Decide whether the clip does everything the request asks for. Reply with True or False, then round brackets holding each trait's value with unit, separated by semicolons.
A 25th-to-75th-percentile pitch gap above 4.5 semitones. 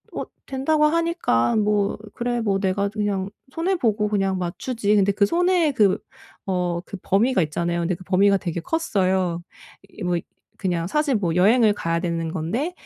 True (5.4 semitones)